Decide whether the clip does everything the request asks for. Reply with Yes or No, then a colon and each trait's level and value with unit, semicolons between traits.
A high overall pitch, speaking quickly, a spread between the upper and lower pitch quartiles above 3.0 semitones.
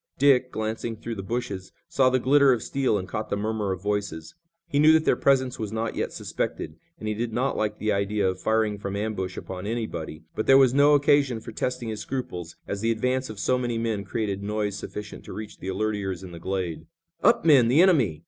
No: low, 110 Hz; fast, 225 wpm; average, 4.2 semitones